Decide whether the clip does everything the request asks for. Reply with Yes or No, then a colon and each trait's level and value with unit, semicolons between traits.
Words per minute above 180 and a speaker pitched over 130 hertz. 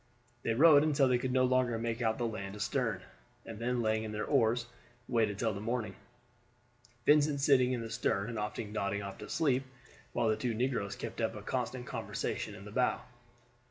No: average, 195 wpm; low, 115 Hz